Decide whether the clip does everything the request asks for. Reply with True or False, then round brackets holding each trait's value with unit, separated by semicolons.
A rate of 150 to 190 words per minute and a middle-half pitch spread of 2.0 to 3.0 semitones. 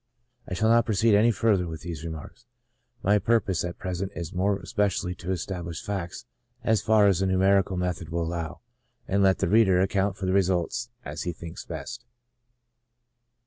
True (175 wpm; 2.7 semitones)